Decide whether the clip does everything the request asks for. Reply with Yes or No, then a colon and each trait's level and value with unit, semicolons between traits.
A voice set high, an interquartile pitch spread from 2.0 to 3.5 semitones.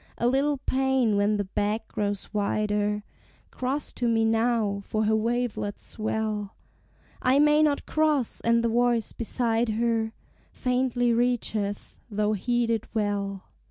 Yes: high, 225 Hz; average, 2.8 semitones